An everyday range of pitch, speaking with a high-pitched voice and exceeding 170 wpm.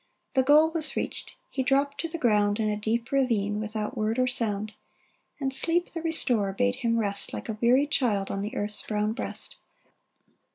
Yes: average, 4.6 semitones; high, 235 Hz; average, 190 wpm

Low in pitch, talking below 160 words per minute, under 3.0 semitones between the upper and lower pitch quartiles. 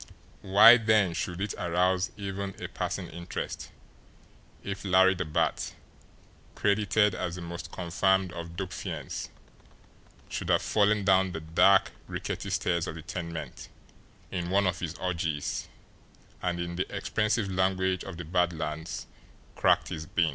Yes: very low, 90 Hz; average, 145 wpm; narrow, 2.4 semitones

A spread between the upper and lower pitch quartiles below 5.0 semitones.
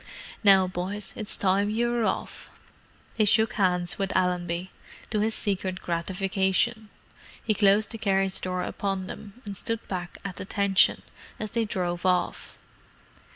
Yes: narrow, 2.5 semitones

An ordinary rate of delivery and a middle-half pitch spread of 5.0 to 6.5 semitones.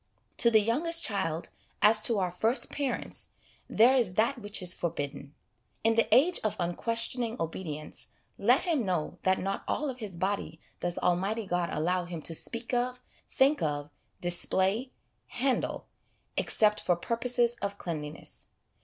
Yes: average, 150 wpm; wide, 5.4 semitones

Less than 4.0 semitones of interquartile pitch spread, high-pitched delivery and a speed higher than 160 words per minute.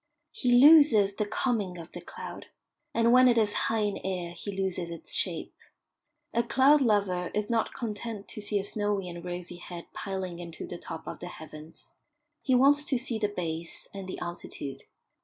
No: average, 4.8 semitones; high, 200 Hz; average, 185 wpm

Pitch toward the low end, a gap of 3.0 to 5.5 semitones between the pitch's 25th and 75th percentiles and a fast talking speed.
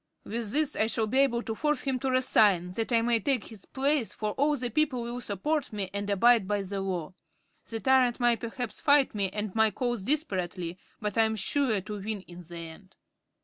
No: high, 225 Hz; average, 4.4 semitones; fast, 215 wpm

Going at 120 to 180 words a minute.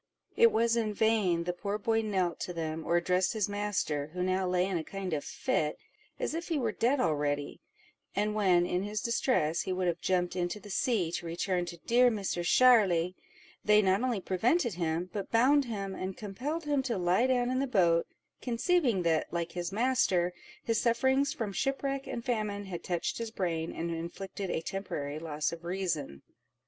No: average, 190 wpm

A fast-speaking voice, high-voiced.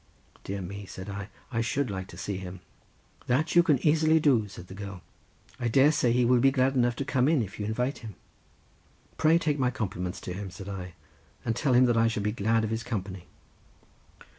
No: fast, 215 wpm; low, 115 Hz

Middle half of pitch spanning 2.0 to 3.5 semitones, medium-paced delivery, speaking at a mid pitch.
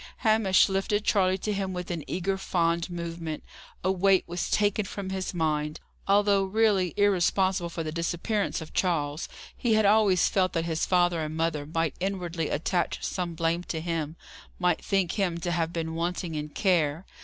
Yes: average, 2.8 semitones; average, 175 wpm; medium, 175 Hz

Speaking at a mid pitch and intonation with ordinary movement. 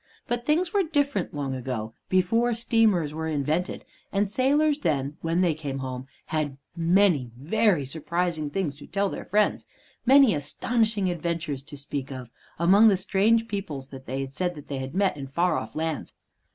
No: medium, 170 Hz; wide, 6.7 semitones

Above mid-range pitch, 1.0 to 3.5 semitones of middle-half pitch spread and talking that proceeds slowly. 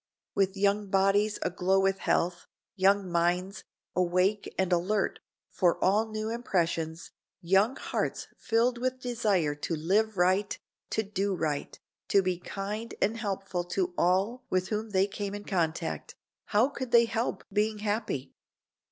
No: high, 195 Hz; average, 2.9 semitones; average, 145 wpm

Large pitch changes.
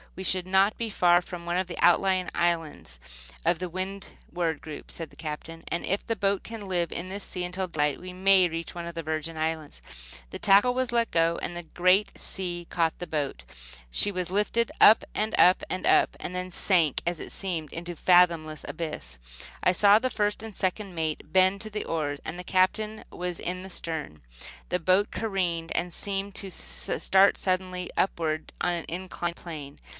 No: average, 2.7 semitones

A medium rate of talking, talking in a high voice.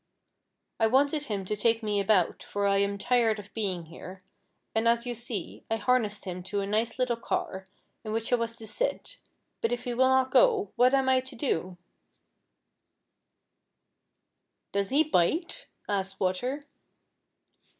Yes: average, 170 wpm; high, 225 Hz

